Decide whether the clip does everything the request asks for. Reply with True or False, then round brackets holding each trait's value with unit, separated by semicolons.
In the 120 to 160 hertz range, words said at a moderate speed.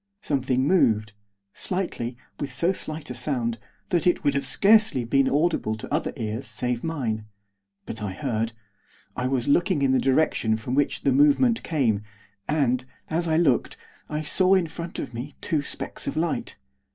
True (135 Hz; 170 wpm)